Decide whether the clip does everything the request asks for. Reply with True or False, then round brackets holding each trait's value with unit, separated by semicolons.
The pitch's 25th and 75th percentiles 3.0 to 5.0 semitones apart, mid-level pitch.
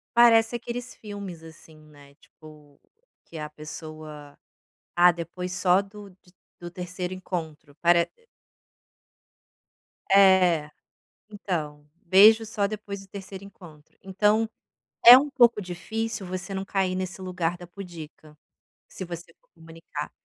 True (3.7 semitones; 180 Hz)